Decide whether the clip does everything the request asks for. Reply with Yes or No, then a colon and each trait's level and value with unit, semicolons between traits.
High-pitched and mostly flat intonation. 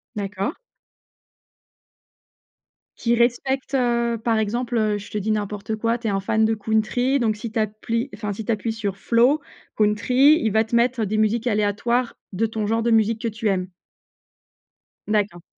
Yes: high, 220 Hz; narrow, 2.1 semitones